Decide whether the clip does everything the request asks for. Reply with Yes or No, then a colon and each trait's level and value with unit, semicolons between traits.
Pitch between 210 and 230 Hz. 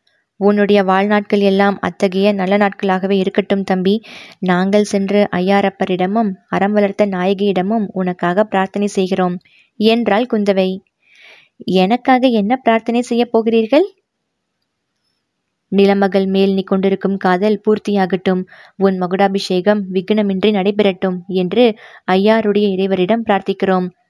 No: high, 200 Hz